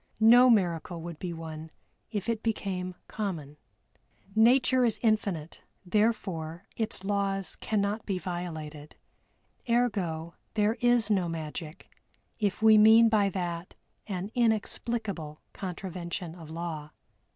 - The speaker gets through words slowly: Yes, slow, 115 wpm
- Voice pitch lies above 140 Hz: Yes, high, 190 Hz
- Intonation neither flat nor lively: Yes, average, 4.5 semitones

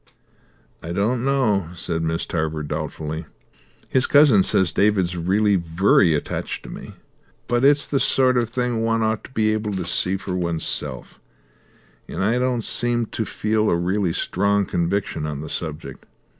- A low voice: Yes, low, 100 Hz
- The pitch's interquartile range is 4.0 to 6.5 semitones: Yes, average, 5.3 semitones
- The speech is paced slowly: No, average, 160 wpm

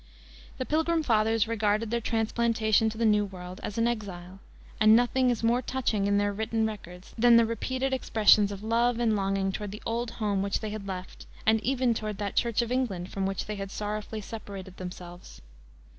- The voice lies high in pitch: Yes, high, 215 Hz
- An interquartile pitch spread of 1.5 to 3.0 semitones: Yes, average, 2.7 semitones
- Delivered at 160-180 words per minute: No, average, 195 wpm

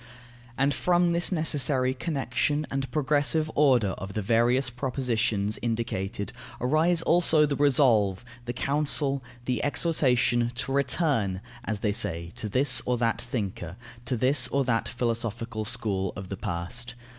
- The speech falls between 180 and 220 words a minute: No, average, 140 wpm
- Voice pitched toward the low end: Yes, low, 125 Hz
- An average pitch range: Yes, average, 4.5 semitones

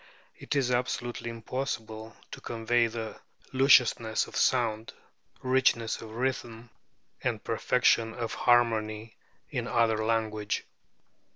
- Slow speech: Yes, slow, 105 wpm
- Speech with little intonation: Yes, narrow, 1.5 semitones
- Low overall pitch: Yes, low, 115 Hz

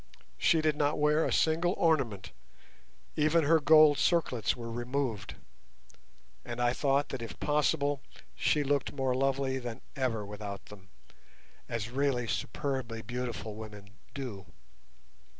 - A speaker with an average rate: No, slow, 130 wpm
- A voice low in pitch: Yes, low, 130 Hz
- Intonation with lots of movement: No, average, 4.3 semitones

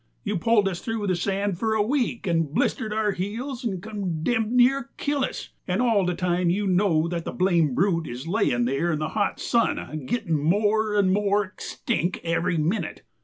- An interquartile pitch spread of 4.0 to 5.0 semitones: Yes, average, 4.4 semitones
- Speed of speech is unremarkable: Yes, average, 190 wpm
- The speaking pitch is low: No, high, 195 Hz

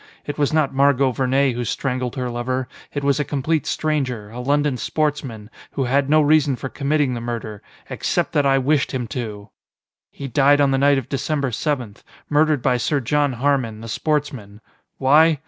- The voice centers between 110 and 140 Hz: Yes, low, 135 Hz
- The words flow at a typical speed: Yes, average, 180 wpm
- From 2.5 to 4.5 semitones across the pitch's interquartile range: Yes, average, 2.9 semitones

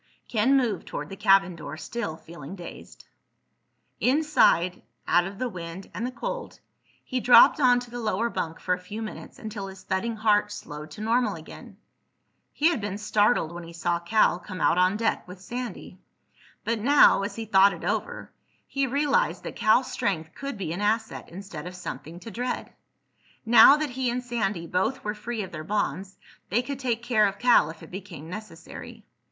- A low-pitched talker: No, high, 210 Hz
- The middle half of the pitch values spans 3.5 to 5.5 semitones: Yes, average, 5.0 semitones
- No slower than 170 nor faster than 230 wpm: Yes, average, 180 wpm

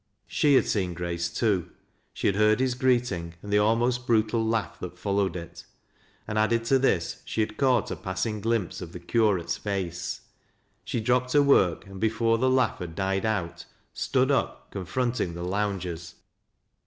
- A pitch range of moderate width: Yes, average, 4.4 semitones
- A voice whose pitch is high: No, low, 105 Hz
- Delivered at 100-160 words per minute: No, average, 175 wpm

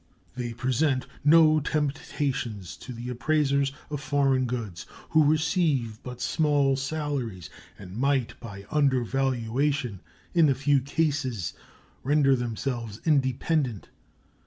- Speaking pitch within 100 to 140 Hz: Yes, low, 135 Hz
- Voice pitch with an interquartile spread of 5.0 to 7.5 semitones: No, average, 3.6 semitones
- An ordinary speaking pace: No, slow, 110 wpm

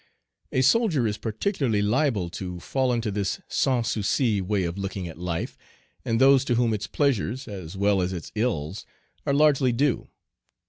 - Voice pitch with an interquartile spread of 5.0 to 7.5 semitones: Yes, average, 5.3 semitones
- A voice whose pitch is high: No, low, 110 Hz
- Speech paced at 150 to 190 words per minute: Yes, average, 170 wpm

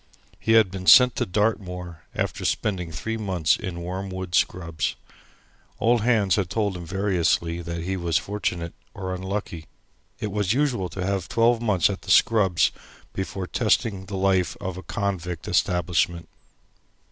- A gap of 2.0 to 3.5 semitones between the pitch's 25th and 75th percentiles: Yes, average, 3.0 semitones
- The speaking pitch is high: No, very low, 95 Hz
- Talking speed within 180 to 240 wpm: No, average, 150 wpm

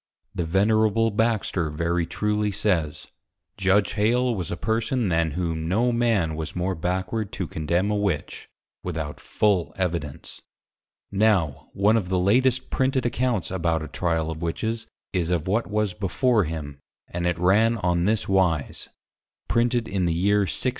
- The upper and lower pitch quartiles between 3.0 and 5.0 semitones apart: Yes, average, 4.6 semitones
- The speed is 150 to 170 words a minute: Yes, average, 155 wpm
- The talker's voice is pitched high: No, very low, 95 Hz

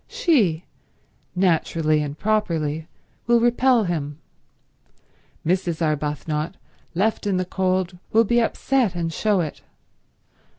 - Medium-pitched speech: Yes, medium, 180 Hz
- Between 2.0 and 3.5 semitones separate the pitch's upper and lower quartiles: No, wide, 5.5 semitones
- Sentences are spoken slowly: Yes, slow, 110 wpm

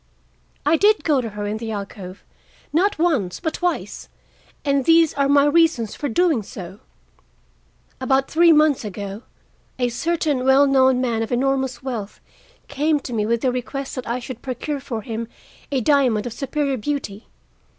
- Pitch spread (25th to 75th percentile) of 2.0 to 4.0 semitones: No, average, 4.4 semitones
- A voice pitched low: No, very high, 265 Hz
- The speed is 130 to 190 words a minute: Yes, average, 165 wpm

